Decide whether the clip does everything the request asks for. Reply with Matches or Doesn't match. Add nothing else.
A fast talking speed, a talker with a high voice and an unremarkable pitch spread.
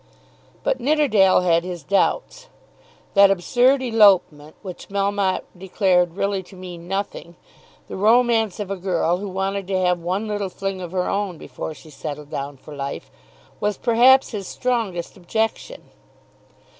Doesn't match